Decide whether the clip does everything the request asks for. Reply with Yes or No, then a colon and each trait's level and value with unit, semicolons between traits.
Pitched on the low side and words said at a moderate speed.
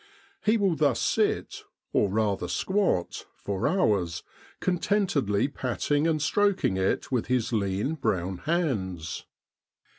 No: low, 125 Hz; slow, 115 wpm